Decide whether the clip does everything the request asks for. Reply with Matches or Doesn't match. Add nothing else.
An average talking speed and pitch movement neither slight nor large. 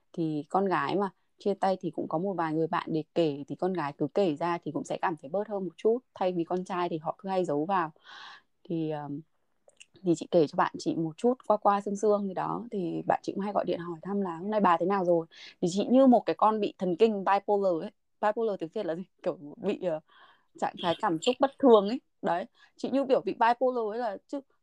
Doesn't match